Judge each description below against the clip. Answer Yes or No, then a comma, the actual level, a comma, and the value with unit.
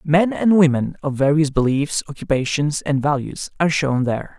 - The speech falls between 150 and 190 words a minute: Yes, average, 165 wpm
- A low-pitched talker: No, medium, 145 Hz